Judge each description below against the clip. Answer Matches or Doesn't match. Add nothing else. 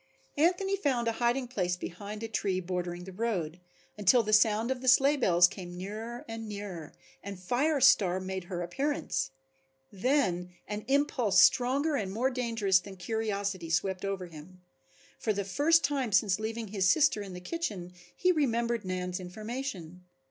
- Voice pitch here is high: Matches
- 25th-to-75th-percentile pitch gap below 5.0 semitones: Doesn't match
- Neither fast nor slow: Matches